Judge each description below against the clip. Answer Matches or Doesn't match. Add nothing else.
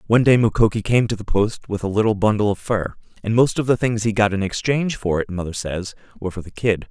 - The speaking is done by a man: Matches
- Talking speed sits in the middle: Doesn't match